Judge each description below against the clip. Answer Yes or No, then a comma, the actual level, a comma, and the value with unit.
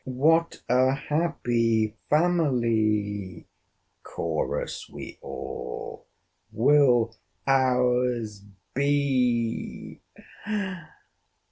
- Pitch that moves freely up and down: No, average, 3.9 semitones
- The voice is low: Yes, low, 125 Hz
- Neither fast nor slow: No, slow, 50 wpm